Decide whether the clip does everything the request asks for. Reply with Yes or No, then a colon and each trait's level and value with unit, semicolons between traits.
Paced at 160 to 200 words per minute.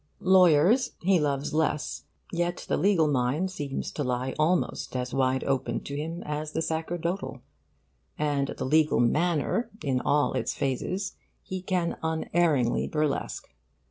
No: average, 140 wpm